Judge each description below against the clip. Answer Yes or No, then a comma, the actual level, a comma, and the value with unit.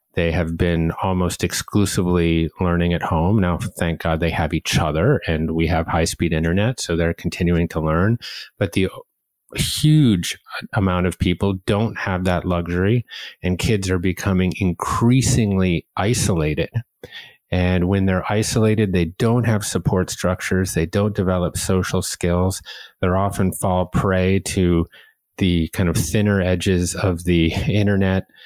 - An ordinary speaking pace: Yes, average, 145 wpm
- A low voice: Yes, very low, 90 Hz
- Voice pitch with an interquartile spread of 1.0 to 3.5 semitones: Yes, average, 2.9 semitones